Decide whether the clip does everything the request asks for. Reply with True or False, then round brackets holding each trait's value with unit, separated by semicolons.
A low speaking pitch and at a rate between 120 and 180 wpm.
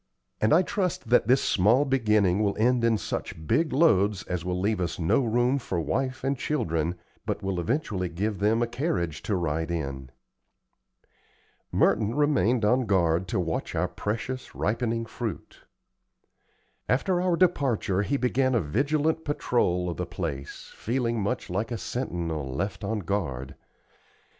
True (105 Hz; 155 wpm)